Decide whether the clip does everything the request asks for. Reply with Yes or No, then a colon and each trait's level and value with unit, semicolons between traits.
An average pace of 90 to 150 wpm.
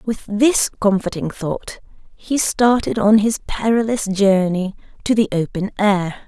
Yes: slow, 135 wpm